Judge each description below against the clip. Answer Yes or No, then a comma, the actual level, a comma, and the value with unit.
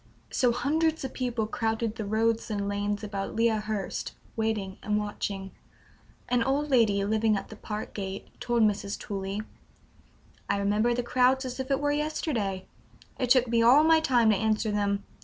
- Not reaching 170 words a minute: No, average, 175 wpm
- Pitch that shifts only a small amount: No, average, 3.3 semitones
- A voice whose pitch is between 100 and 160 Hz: No, high, 220 Hz